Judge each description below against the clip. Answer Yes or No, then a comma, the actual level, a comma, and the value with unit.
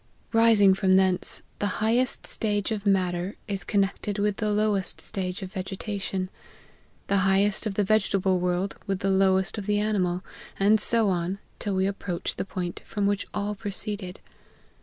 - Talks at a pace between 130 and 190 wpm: Yes, average, 170 wpm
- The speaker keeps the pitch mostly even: Yes, narrow, 1.7 semitones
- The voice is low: No, high, 195 Hz